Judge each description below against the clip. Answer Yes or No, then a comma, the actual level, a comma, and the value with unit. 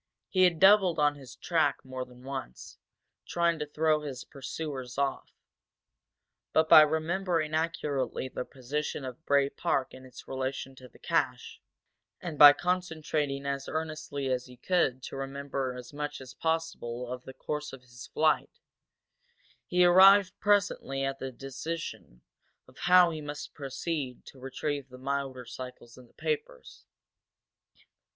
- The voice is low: No, medium, 145 Hz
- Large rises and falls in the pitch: No, average, 3.6 semitones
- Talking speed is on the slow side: No, average, 145 wpm